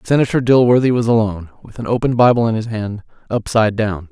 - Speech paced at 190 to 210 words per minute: No, average, 175 wpm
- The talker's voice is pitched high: No, low, 115 Hz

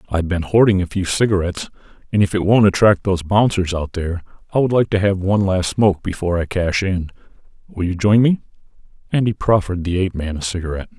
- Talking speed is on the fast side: Yes, fast, 220 wpm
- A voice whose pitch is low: Yes, very low, 95 Hz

